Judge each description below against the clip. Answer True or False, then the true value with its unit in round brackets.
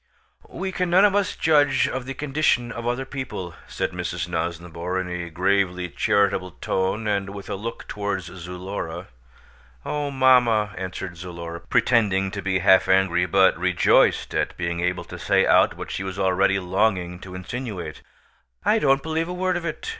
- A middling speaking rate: True (170 wpm)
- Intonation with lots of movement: True (5.8 semitones)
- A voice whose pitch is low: True (95 Hz)